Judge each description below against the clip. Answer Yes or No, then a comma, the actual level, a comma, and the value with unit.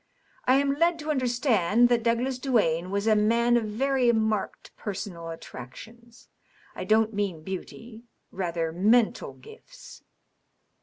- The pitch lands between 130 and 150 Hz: No, high, 225 Hz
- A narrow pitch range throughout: No, average, 3.9 semitones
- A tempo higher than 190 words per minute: No, slow, 135 wpm